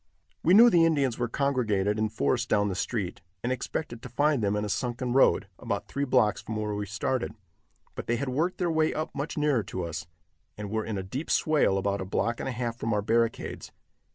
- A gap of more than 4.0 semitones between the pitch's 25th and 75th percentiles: Yes, average, 5.1 semitones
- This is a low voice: Yes, low, 120 Hz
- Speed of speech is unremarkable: No, fast, 225 wpm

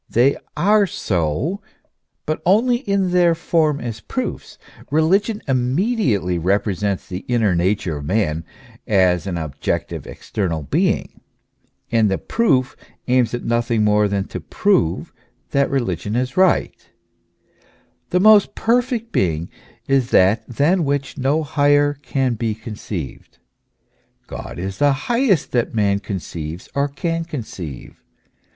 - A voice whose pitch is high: No, low, 125 Hz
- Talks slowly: Yes, slow, 130 wpm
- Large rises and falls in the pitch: Yes, wide, 8.8 semitones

